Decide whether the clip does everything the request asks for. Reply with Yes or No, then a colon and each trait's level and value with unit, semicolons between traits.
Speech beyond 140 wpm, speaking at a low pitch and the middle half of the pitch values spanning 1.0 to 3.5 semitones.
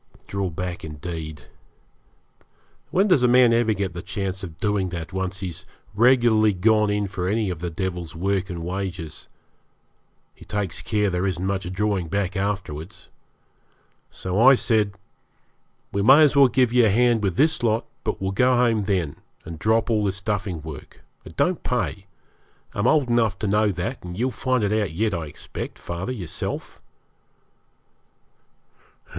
No: average, 165 wpm; low, 100 Hz; average, 4.0 semitones